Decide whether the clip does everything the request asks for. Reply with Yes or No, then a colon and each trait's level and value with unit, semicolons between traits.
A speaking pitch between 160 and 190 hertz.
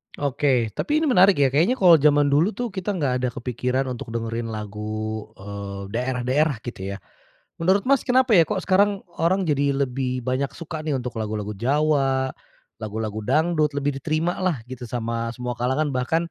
No: low, 135 Hz